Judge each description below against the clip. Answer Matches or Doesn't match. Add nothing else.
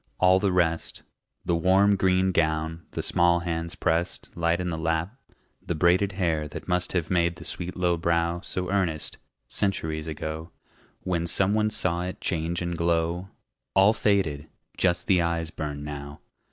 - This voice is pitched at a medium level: Doesn't match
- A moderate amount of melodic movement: Doesn't match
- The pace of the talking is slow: Doesn't match